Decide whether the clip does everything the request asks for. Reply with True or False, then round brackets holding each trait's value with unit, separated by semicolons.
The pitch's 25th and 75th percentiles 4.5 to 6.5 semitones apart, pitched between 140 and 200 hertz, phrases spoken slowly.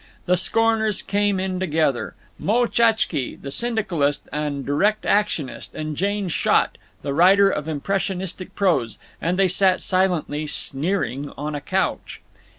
True (5.1 semitones; 185 Hz; 125 wpm)